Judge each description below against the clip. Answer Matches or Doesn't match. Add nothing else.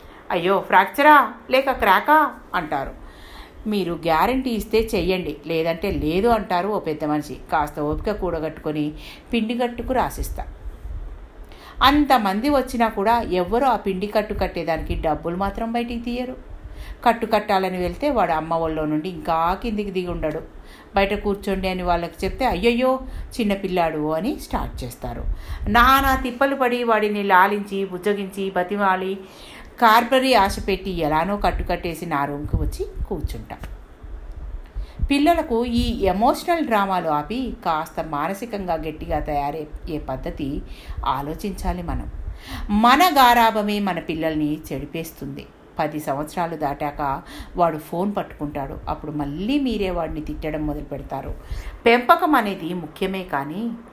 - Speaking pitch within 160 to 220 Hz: Matches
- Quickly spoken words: Doesn't match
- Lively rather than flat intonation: Matches